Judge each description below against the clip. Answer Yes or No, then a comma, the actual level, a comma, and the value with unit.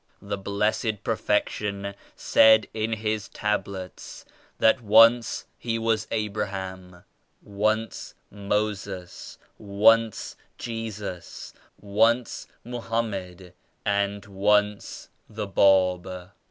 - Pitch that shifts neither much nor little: No, narrow, 2.2 semitones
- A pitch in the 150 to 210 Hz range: No, low, 105 Hz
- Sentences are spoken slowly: Yes, slow, 85 wpm